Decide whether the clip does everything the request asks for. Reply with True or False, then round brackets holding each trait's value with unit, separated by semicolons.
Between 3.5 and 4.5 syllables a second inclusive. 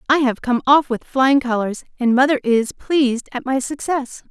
False (4.7 syllables/s)